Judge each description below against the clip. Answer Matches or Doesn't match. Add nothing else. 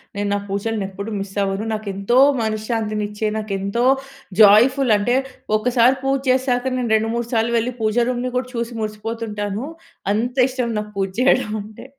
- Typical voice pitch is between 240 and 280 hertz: Doesn't match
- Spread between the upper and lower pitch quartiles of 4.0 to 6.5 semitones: Doesn't match